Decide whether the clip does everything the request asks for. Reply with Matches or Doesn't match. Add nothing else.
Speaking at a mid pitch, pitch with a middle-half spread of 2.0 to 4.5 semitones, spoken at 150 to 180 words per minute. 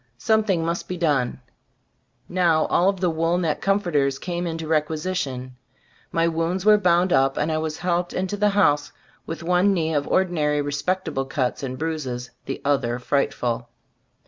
Matches